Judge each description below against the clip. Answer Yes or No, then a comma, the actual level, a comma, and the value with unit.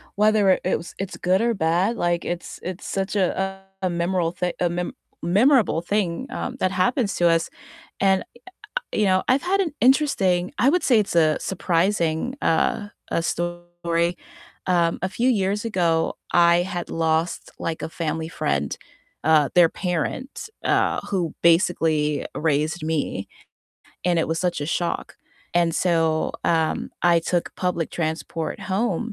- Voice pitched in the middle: Yes, medium, 175 Hz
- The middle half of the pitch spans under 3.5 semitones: Yes, average, 2.9 semitones